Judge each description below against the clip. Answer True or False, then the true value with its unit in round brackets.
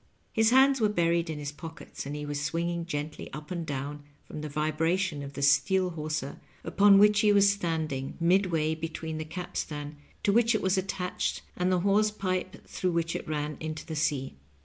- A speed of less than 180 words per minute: False (195 wpm)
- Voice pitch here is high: False (165 Hz)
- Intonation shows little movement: False (3.9 semitones)